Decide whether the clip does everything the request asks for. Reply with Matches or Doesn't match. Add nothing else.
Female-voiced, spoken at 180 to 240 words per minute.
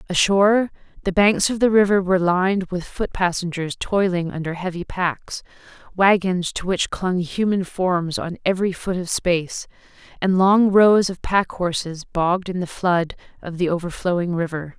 Doesn't match